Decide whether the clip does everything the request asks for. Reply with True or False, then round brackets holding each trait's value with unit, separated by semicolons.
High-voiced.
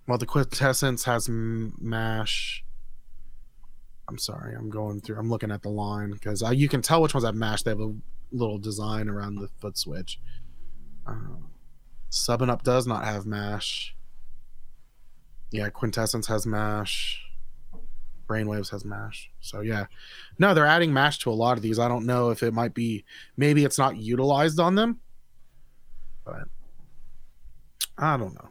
False (115 Hz)